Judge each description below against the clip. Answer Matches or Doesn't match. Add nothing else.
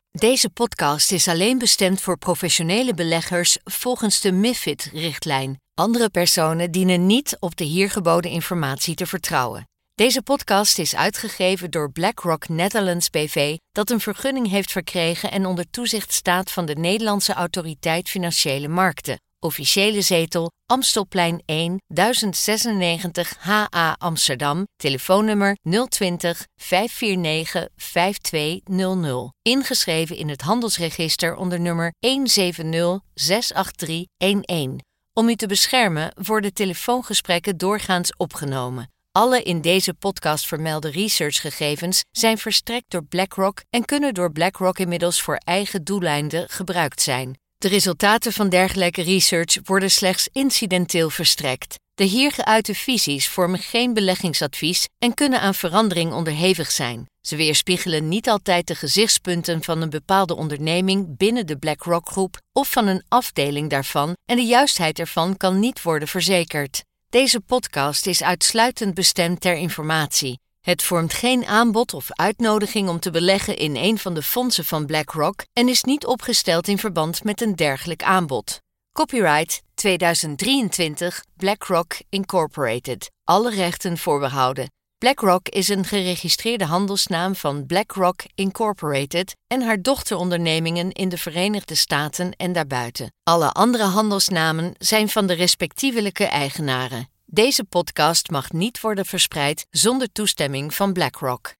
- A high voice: Doesn't match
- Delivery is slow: Matches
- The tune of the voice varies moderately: Matches